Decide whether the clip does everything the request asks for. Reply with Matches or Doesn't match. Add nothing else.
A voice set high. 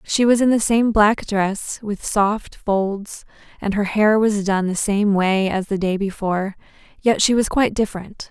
Matches